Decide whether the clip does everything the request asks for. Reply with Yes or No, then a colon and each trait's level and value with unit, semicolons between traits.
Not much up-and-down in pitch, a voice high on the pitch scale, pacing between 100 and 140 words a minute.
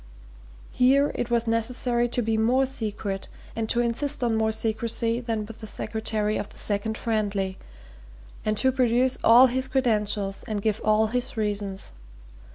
No: narrow, 2.3 semitones; high, 225 Hz; average, 160 wpm